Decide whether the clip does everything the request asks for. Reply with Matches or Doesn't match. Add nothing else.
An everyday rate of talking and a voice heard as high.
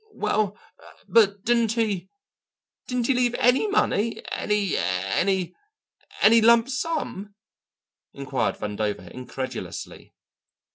Doesn't match